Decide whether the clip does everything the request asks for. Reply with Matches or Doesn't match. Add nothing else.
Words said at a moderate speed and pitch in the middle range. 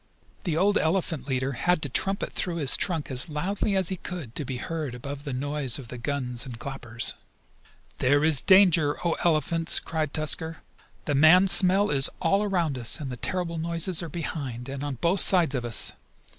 Matches